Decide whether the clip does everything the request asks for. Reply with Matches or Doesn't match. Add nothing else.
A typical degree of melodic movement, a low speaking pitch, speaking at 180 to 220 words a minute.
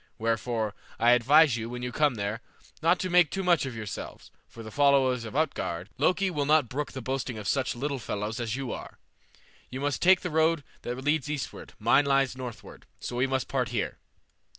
Matches